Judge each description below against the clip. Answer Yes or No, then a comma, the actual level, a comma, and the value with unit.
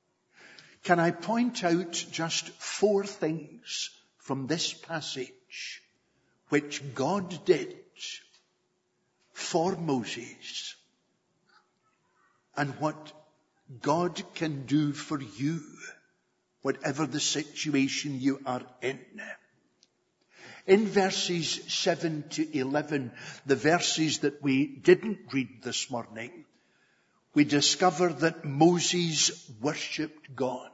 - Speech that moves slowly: Yes, slow, 90 wpm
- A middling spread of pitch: Yes, average, 3.9 semitones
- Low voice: No, medium, 155 Hz